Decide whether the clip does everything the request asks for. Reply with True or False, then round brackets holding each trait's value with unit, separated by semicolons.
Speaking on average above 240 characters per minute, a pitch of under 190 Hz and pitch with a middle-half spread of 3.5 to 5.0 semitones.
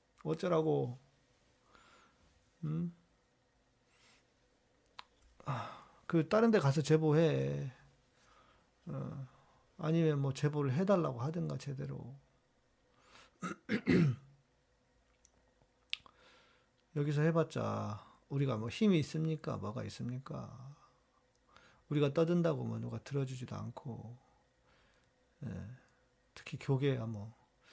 False (170 characters per minute; 135 Hz; 4.0 semitones)